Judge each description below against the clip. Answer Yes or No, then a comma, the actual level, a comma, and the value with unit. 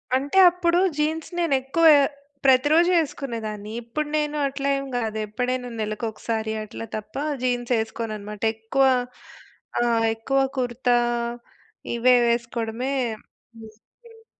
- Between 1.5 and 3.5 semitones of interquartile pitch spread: No, average, 4.6 semitones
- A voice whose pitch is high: Yes, very high, 250 Hz